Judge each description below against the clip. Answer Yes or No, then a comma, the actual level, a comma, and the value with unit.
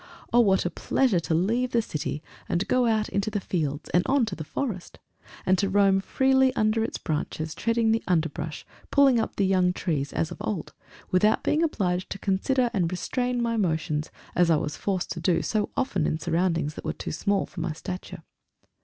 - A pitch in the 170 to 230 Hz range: Yes, high, 190 Hz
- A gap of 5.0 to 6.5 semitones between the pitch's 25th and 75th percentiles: Yes, average, 5.3 semitones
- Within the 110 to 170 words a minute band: No, average, 200 wpm